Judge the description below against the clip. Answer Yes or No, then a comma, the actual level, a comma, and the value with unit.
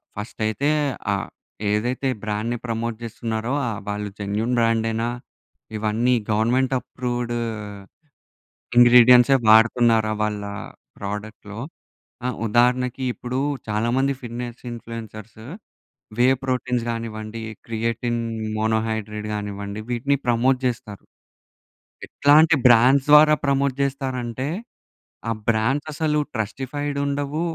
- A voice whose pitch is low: Yes, low, 115 Hz